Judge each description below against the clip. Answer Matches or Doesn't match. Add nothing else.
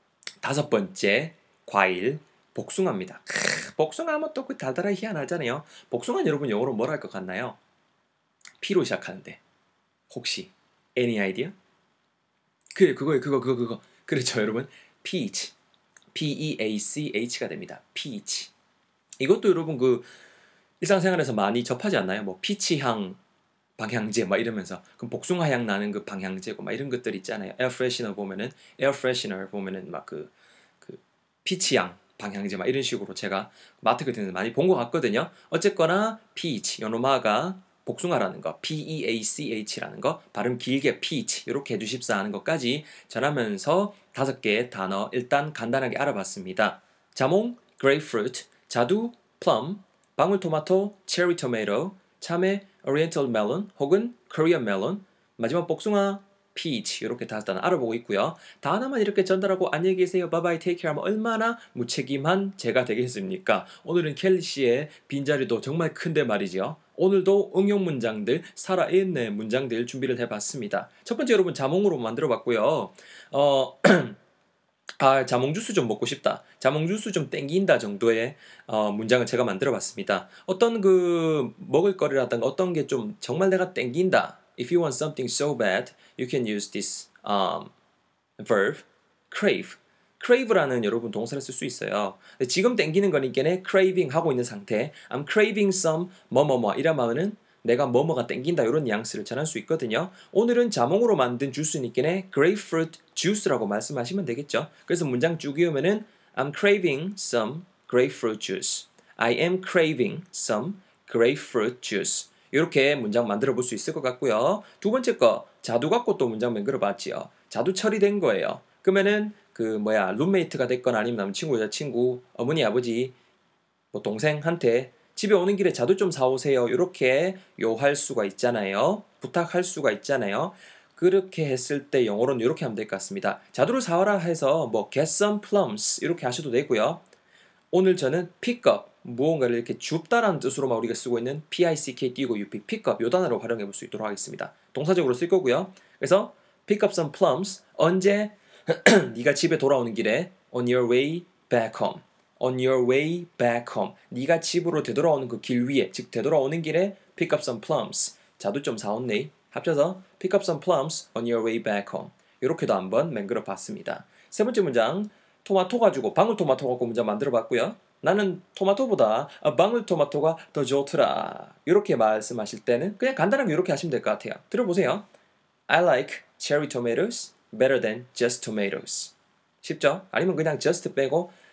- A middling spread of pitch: Doesn't match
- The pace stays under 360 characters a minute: Doesn't match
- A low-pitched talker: Doesn't match